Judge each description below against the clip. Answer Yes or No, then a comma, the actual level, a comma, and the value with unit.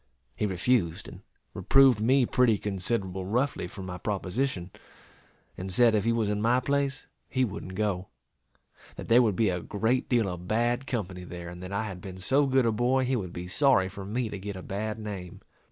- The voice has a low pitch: Yes, low, 105 Hz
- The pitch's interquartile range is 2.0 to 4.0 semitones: No, average, 4.7 semitones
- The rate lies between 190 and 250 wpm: Yes, average, 200 wpm